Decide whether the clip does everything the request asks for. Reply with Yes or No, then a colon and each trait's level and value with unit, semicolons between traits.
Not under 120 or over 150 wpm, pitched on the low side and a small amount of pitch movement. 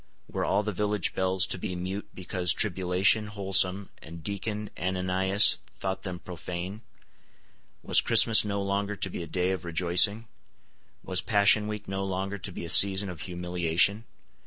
No: average, 160 wpm; very low, 95 Hz; narrow, 2.1 semitones